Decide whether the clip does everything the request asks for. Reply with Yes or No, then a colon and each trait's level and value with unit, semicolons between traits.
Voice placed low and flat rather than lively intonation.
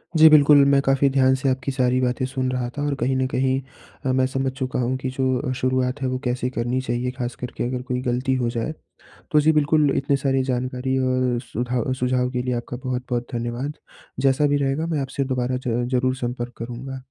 Yes: low, 130 Hz; narrow, 1.2 semitones